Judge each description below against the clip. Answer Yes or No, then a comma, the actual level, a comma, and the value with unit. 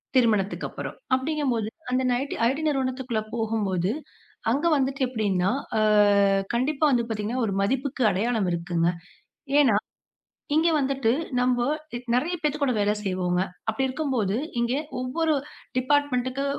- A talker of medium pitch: No, very high, 250 Hz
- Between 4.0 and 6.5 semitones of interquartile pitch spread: Yes, average, 4.5 semitones